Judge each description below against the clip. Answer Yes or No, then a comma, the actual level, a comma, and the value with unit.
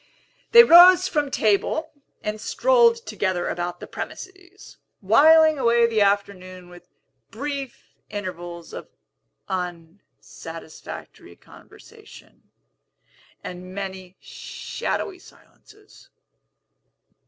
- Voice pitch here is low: No, high, 210 Hz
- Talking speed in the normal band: No, slow, 85 wpm